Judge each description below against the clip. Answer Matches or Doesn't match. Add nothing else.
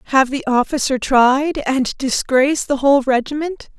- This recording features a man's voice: Doesn't match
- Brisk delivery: Doesn't match